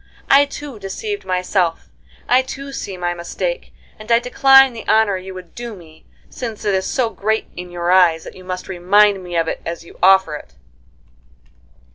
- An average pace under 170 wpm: No, average, 185 wpm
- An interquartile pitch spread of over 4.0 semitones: Yes, average, 5.2 semitones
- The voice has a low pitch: No, high, 190 Hz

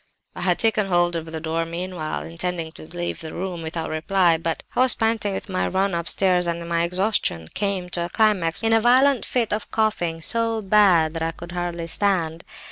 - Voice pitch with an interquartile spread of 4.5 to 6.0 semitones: No, average, 3.6 semitones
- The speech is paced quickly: Yes, fast, 210 wpm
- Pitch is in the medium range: Yes, medium, 175 Hz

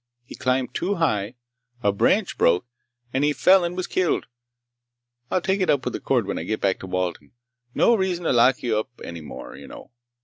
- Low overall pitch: Yes, low, 130 Hz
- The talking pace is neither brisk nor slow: No, fast, 210 wpm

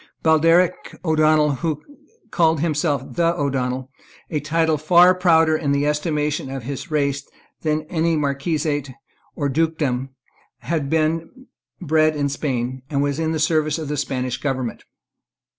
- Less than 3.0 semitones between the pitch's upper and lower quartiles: Yes, narrow, 2.4 semitones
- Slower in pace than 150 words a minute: Yes, average, 140 wpm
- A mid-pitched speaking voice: Yes, medium, 150 Hz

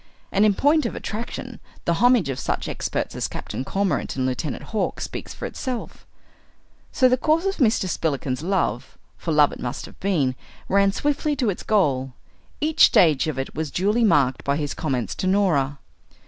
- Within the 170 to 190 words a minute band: Yes, average, 180 wpm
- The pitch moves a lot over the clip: Yes, wide, 8.6 semitones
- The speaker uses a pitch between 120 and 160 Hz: No, medium, 185 Hz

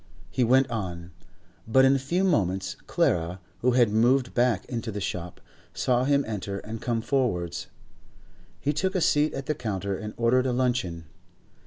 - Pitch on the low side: Yes, low, 120 Hz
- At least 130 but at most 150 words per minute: No, average, 170 wpm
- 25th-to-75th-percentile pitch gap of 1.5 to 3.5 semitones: No, average, 5.0 semitones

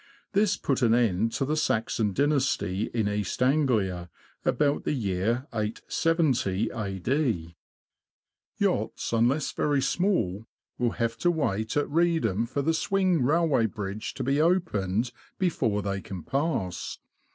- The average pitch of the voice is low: Yes, low, 120 Hz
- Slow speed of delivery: Yes, slow, 130 wpm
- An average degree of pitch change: No, wide, 6.5 semitones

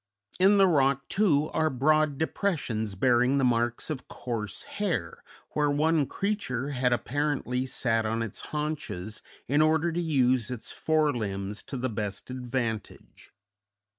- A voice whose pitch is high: No, low, 130 Hz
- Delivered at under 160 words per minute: Yes, average, 140 wpm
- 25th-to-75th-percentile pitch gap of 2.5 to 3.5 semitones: No, average, 4.9 semitones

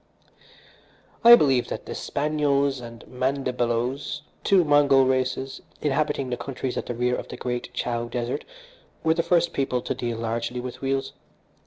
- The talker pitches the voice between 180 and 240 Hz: No, low, 130 Hz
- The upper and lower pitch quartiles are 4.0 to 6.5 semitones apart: No, average, 2.7 semitones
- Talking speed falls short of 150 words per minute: No, average, 155 wpm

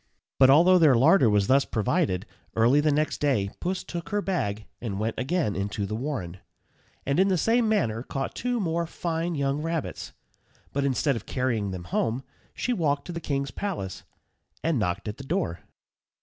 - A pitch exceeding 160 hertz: No, medium, 140 Hz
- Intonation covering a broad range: Yes, wide, 7.4 semitones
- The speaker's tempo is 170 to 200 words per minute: Yes, average, 180 wpm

